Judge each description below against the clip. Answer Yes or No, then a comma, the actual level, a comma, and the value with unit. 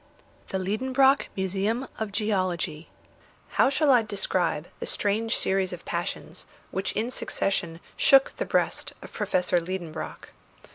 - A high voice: Yes, high, 195 Hz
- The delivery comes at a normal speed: No, slow, 130 wpm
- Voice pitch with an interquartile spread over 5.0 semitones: No, average, 3.9 semitones